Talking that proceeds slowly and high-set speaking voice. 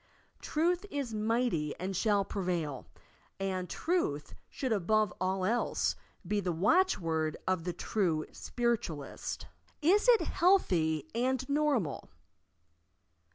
Yes: slow, 110 wpm; high, 200 Hz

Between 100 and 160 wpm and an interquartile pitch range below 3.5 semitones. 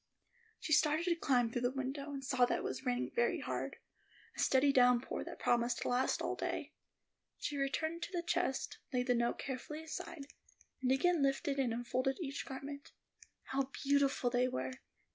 No: average, 180 wpm; average, 2.9 semitones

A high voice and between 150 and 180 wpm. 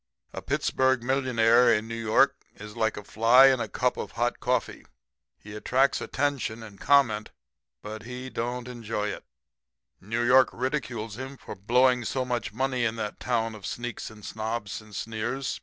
No: low, 120 Hz; average, 170 wpm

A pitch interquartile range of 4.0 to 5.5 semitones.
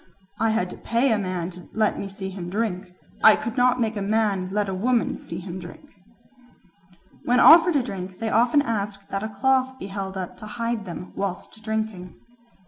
No: average, 3.5 semitones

